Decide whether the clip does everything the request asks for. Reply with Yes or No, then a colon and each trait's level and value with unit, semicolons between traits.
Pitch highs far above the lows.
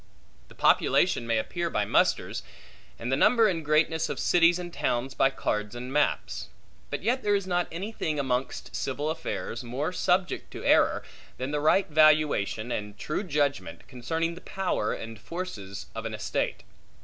Yes: wide, 6.2 semitones